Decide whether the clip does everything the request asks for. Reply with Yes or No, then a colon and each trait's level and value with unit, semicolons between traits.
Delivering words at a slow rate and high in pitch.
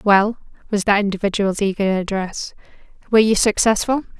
Yes: slow, 130 wpm; high, 205 Hz